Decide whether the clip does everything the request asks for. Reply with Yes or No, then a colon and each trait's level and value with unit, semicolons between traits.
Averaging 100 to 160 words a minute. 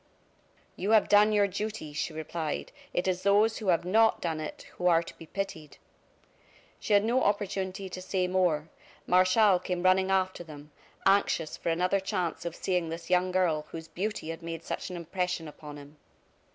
No: average, 180 wpm